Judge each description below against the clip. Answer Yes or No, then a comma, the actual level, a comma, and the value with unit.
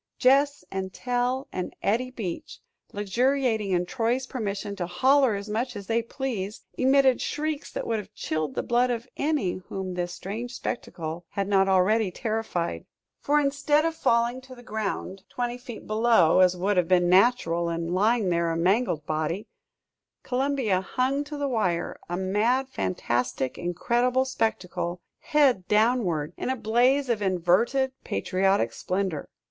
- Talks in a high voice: Yes, high, 215 Hz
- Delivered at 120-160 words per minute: Yes, average, 150 wpm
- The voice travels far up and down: Yes, wide, 5.7 semitones